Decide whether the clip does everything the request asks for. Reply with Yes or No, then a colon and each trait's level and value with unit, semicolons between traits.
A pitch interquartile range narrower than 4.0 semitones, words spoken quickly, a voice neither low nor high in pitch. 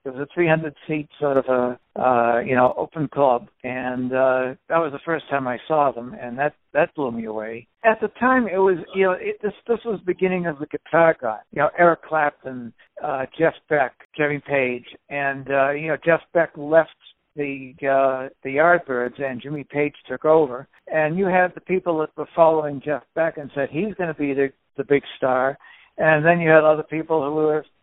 Yes: average, 3.5 semitones; fast, 215 wpm; medium, 150 Hz